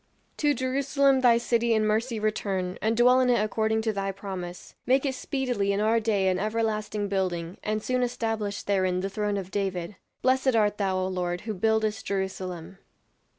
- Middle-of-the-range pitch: No, high, 215 Hz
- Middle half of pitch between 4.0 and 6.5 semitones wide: No, average, 3.4 semitones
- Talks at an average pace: Yes, average, 180 wpm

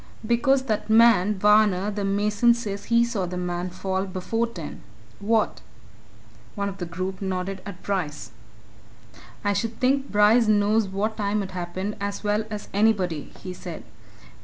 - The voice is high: Yes, high, 205 Hz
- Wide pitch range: No, average, 2.8 semitones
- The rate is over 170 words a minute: No, average, 155 wpm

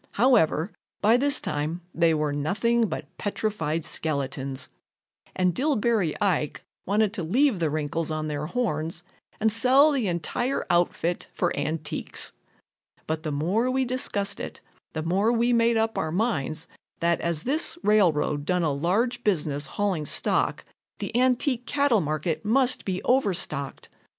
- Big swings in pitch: Yes, wide, 7.1 semitones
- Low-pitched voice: No, medium, 185 Hz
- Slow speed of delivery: No, average, 145 wpm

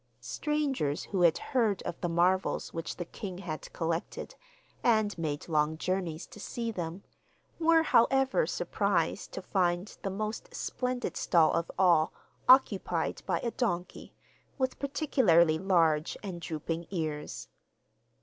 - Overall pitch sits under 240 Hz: Yes, medium, 185 Hz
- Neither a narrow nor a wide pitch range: No, wide, 5.9 semitones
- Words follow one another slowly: Yes, slow, 130 wpm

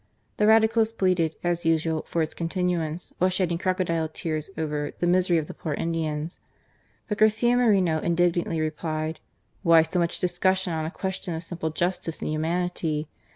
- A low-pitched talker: No, medium, 170 Hz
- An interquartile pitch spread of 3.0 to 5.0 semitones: No, narrow, 2.5 semitones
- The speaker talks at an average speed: Yes, average, 160 wpm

